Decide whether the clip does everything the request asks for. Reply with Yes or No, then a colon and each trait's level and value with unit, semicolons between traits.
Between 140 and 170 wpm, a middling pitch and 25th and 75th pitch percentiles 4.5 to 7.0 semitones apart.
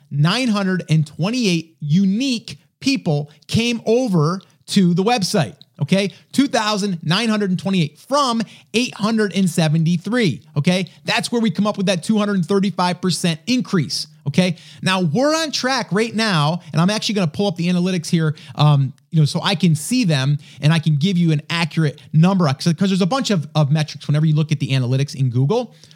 Yes: average, 160 wpm; medium, 175 Hz; average, 4.8 semitones